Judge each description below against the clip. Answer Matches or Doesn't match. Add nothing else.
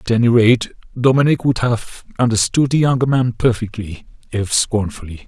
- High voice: Doesn't match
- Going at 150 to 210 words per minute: Doesn't match